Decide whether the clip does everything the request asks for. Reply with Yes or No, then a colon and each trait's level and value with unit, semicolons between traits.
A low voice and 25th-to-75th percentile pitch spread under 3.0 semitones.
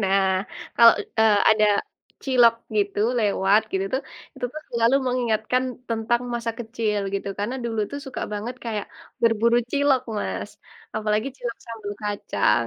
No: high, 225 Hz; narrow, 2.5 semitones